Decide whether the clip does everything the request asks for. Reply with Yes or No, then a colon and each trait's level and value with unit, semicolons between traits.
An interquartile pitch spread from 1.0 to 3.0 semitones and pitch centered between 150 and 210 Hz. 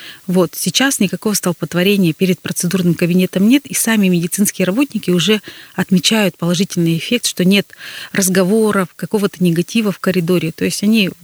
Yes: narrow, 2.5 semitones; medium, 185 Hz